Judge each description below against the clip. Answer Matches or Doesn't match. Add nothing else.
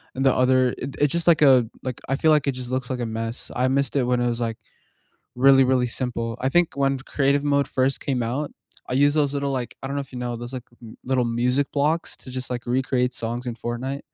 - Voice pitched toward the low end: Matches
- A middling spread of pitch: Doesn't match